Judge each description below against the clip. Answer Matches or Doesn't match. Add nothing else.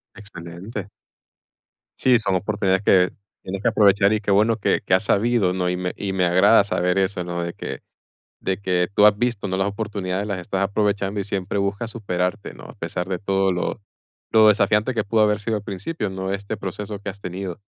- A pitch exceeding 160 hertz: Doesn't match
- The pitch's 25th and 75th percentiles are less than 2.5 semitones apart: Matches